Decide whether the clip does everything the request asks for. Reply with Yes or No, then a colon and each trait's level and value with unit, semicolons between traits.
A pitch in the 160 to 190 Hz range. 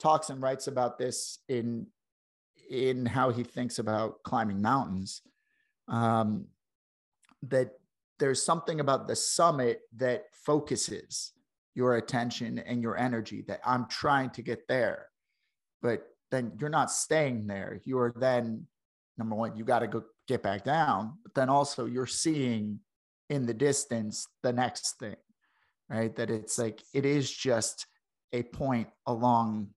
No: low, 125 Hz